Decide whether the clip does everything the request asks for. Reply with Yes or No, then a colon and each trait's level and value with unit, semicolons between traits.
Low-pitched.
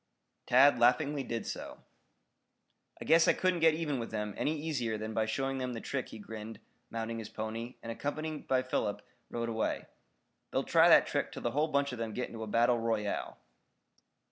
Yes: low, 120 Hz